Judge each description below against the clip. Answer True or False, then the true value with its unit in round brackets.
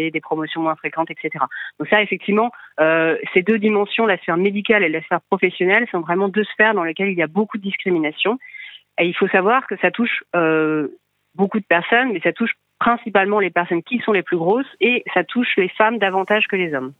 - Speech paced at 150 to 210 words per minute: False (220 wpm)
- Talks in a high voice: True (195 Hz)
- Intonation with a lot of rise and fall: False (4.4 semitones)